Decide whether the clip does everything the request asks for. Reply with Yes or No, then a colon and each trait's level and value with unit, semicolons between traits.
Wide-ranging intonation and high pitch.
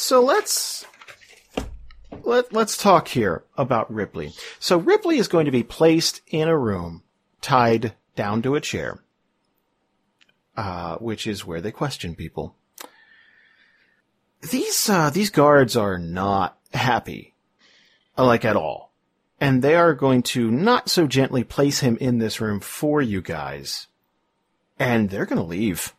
No: wide, 7.5 semitones; low, 135 Hz